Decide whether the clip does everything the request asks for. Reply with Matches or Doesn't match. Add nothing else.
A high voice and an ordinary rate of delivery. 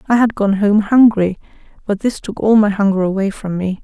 Doesn't match